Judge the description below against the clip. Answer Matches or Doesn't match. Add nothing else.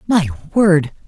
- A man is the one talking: Doesn't match